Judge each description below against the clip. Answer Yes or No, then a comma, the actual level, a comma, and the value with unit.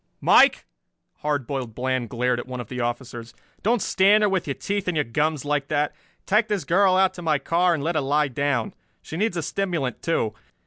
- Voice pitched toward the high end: No, medium, 150 Hz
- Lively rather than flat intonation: Yes, wide, 6.1 semitones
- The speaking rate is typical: No, fast, 215 wpm